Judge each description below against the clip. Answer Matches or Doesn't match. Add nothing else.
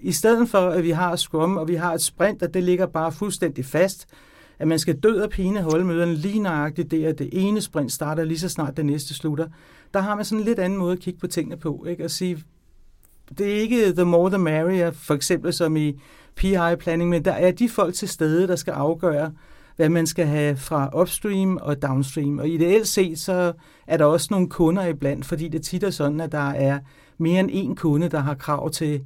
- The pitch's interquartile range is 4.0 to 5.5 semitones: Doesn't match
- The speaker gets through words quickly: Matches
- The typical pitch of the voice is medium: Matches